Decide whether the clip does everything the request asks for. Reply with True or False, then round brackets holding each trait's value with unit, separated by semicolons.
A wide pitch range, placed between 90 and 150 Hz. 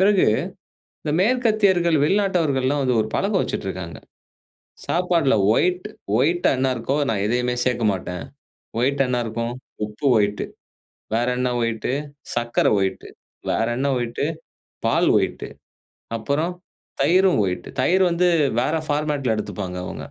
True (7.1 semitones; 135 Hz)